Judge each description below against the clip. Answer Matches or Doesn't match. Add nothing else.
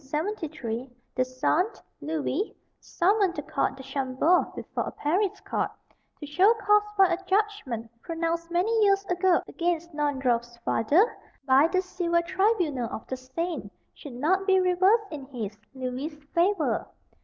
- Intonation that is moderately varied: Doesn't match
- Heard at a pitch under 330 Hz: Doesn't match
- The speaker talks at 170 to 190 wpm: Doesn't match